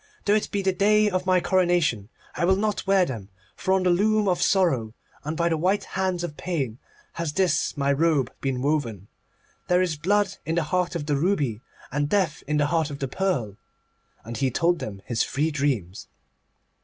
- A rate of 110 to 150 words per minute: No, average, 200 wpm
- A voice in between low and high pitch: Yes, medium, 165 Hz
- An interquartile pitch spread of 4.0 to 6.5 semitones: Yes, average, 5.1 semitones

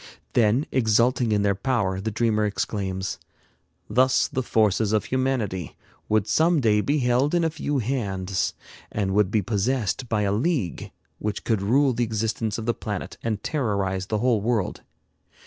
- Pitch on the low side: Yes, low, 110 Hz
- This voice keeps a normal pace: Yes, average, 165 wpm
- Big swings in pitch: No, average, 3.8 semitones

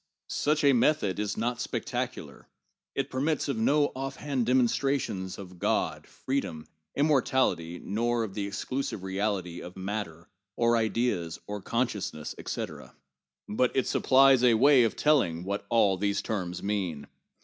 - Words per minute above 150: No, average, 140 wpm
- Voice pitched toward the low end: Yes, low, 110 Hz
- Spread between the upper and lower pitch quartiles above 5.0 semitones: Yes, wide, 5.6 semitones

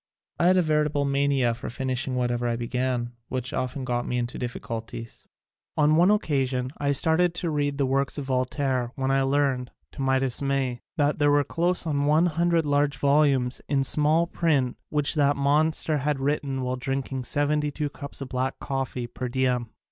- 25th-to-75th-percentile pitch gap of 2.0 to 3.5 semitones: Yes, narrow, 2.6 semitones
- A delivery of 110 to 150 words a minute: No, average, 180 wpm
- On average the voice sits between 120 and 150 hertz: Yes, medium, 140 Hz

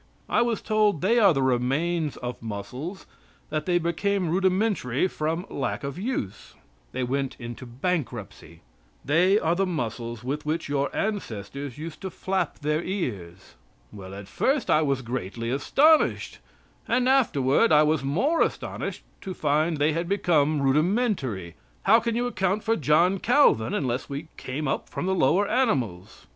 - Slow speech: No, average, 155 wpm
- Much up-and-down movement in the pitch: Yes, wide, 6.9 semitones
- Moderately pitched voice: Yes, medium, 155 Hz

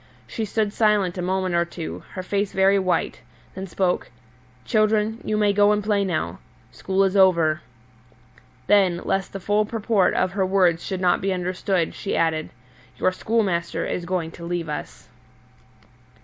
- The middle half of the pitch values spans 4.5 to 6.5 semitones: No, narrow, 2.6 semitones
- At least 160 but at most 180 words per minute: Yes, average, 165 wpm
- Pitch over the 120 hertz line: Yes, high, 190 Hz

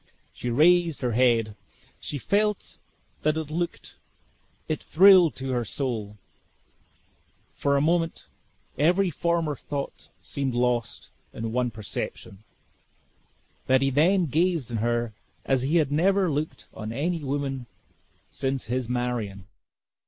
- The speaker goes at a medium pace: No, slow, 125 wpm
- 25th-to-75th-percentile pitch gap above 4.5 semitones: Yes, wide, 5.4 semitones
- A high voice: No, low, 135 Hz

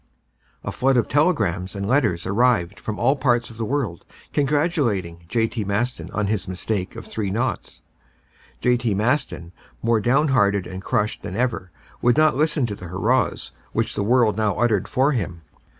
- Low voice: Yes, low, 110 Hz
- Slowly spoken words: No, average, 165 wpm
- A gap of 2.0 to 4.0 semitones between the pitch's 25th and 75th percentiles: No, average, 4.5 semitones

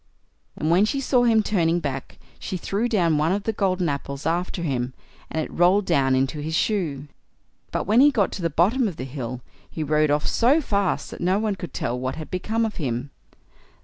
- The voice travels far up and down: Yes, wide, 6.2 semitones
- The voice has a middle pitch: Yes, medium, 170 Hz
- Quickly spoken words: Yes, fast, 215 wpm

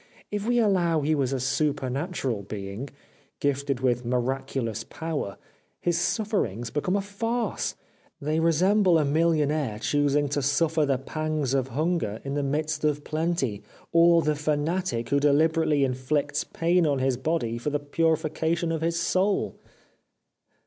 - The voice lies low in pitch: No, medium, 150 Hz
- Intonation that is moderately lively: Yes, average, 3.8 semitones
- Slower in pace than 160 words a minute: Yes, average, 145 wpm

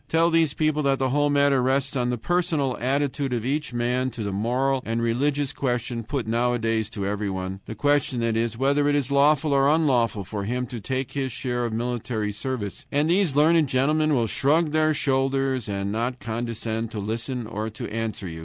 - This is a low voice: Yes, low, 130 Hz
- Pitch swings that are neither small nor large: Yes, average, 3.9 semitones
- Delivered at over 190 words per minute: Yes, average, 200 wpm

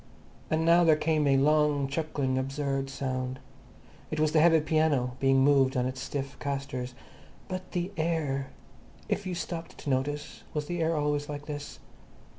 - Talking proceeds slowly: No, average, 165 wpm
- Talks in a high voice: No, medium, 145 Hz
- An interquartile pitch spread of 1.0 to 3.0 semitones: Yes, average, 2.7 semitones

